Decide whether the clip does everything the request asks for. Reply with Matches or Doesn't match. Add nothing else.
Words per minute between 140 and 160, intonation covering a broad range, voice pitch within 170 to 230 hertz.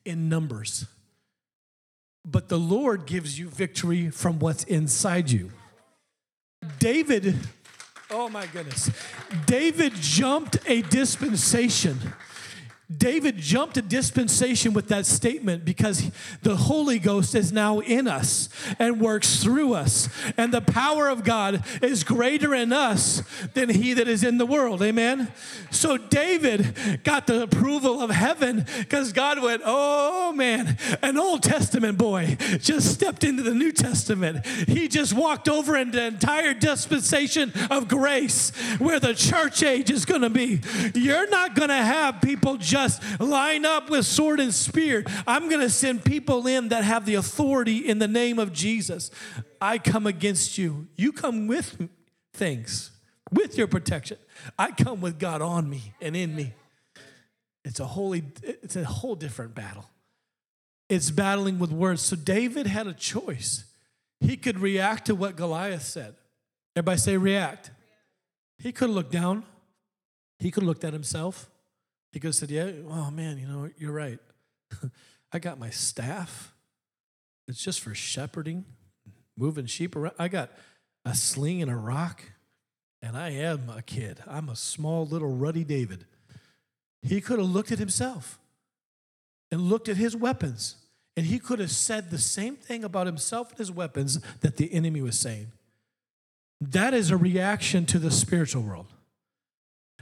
Matches